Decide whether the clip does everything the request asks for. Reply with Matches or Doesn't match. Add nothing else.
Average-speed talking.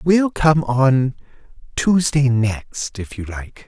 Doesn't match